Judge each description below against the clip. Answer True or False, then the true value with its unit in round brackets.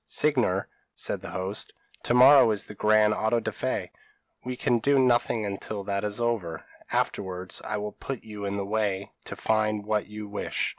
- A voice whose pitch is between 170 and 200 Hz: False (105 Hz)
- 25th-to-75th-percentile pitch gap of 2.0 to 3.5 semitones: True (2.8 semitones)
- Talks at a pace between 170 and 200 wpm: True (190 wpm)